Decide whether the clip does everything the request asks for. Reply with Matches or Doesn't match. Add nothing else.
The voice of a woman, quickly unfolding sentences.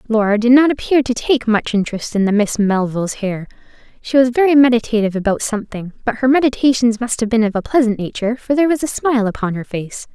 Matches